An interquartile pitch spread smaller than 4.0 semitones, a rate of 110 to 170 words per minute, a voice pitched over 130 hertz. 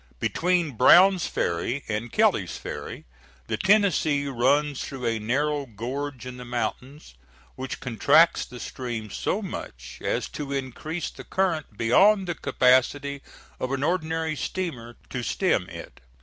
No: average, 4.8 semitones; slow, 135 wpm; medium, 140 Hz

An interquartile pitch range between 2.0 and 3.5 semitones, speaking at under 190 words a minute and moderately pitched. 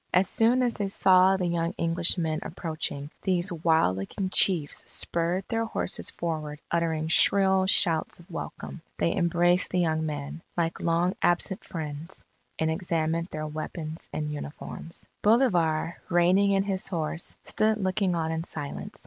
Yes: average, 2.9 semitones; average, 150 wpm; medium, 170 Hz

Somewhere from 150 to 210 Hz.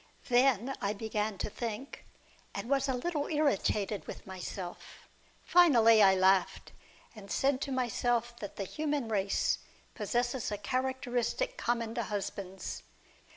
No: high, 235 Hz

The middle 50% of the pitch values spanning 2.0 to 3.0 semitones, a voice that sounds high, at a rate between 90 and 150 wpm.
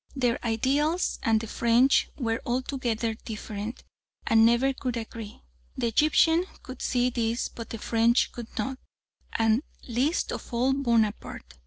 Yes: narrow, 2.5 semitones; high, 235 Hz; average, 140 wpm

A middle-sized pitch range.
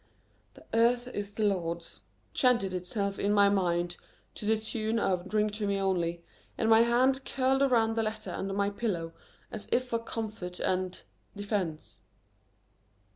Yes: average, 3.6 semitones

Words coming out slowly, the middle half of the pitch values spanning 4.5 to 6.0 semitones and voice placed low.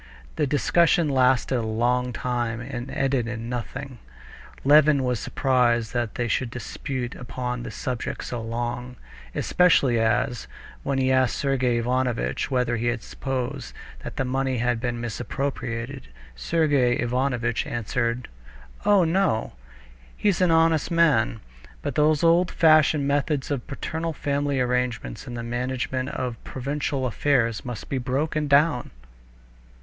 No: slow, 130 wpm; average, 2.9 semitones; low, 125 Hz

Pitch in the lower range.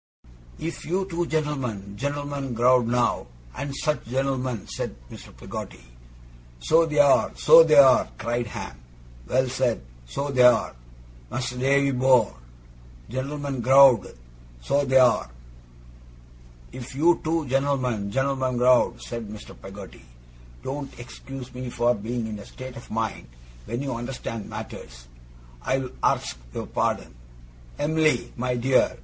Yes: low, 130 Hz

